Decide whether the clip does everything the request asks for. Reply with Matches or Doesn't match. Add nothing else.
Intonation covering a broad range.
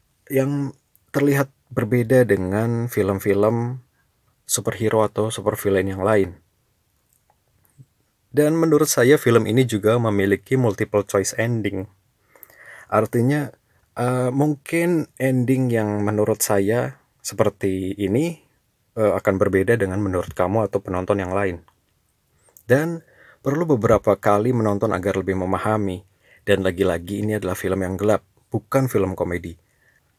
Doesn't match